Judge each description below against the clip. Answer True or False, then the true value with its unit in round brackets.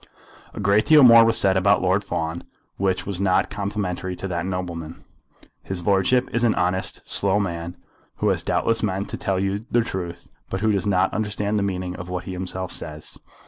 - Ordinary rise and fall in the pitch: False (2.2 semitones)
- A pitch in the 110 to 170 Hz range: False (95 Hz)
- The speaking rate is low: False (195 wpm)